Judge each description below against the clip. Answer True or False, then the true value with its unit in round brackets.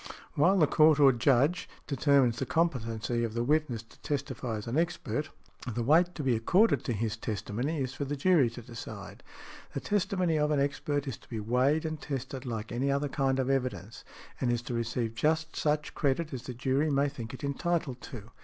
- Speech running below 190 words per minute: False (200 wpm)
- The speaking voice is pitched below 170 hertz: True (135 Hz)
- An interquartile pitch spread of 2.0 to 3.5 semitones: False (4.2 semitones)